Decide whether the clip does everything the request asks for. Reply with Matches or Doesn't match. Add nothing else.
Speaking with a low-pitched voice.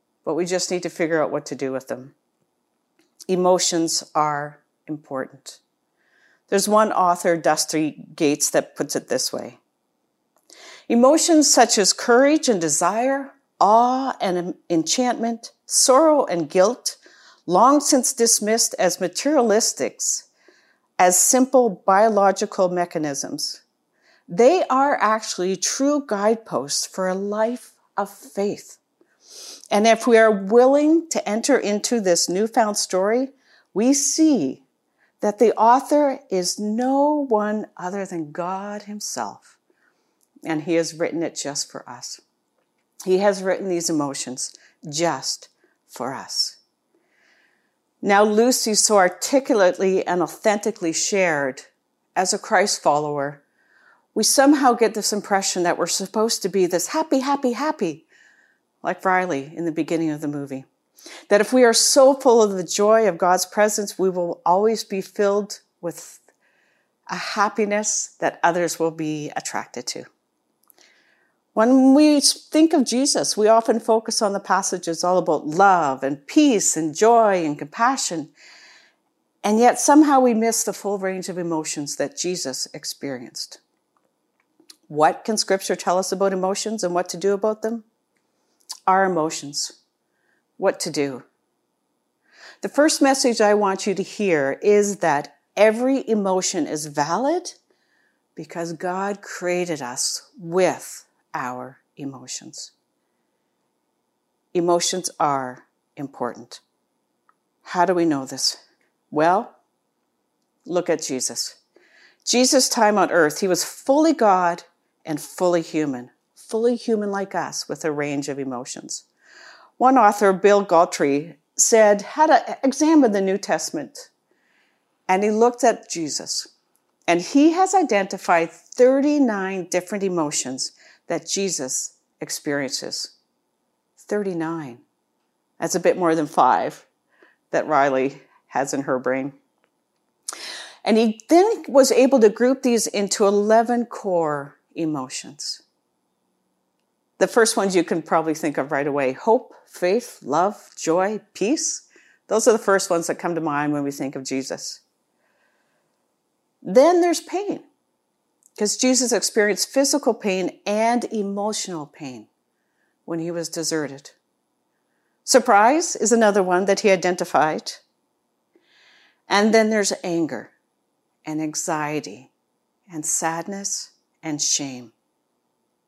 Doesn't match